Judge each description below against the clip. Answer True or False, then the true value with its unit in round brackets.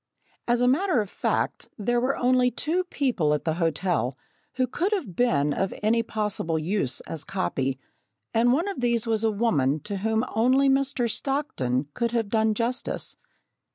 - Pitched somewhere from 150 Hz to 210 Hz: False (225 Hz)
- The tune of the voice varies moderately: False (6.2 semitones)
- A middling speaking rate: True (170 wpm)